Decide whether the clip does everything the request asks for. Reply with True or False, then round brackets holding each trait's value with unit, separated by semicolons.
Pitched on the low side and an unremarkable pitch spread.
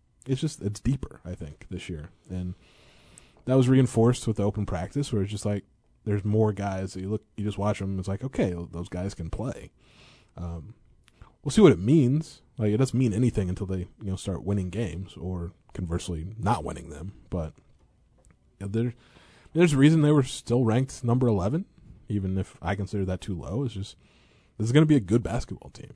True (105 Hz; 4.8 semitones)